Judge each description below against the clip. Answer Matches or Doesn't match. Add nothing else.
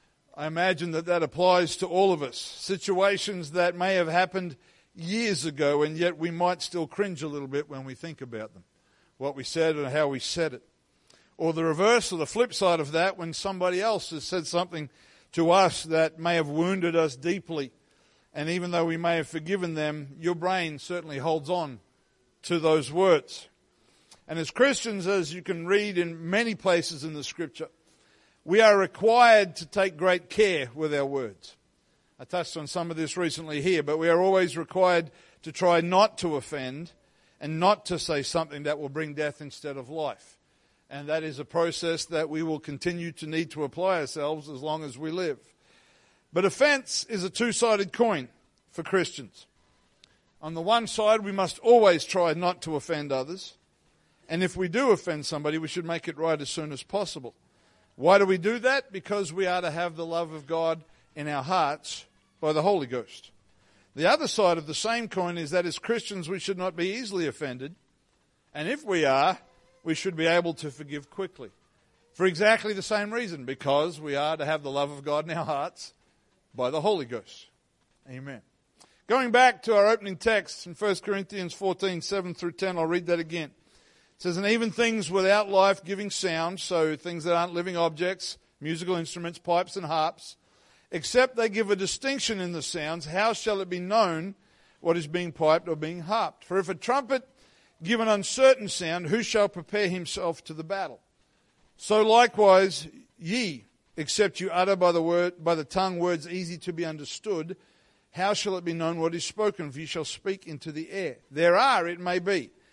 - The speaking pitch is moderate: Matches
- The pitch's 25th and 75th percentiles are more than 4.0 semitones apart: Doesn't match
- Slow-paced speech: Doesn't match